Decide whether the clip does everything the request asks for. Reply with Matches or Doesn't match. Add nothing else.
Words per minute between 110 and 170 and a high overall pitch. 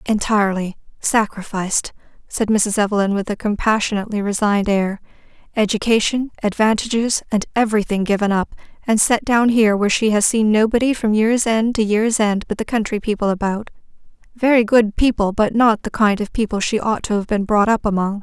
Matches